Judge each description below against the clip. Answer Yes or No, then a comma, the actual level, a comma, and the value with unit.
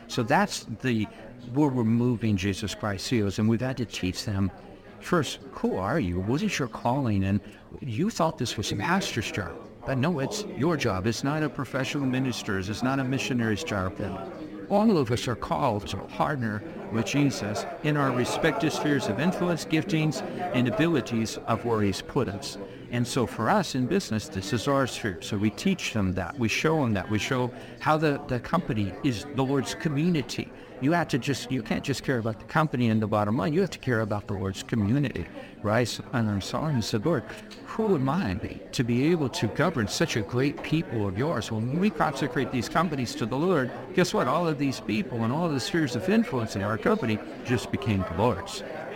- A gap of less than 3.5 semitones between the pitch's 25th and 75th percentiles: No, wide, 5.4 semitones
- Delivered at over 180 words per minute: Yes, fast, 205 wpm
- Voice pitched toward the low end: Yes, low, 125 Hz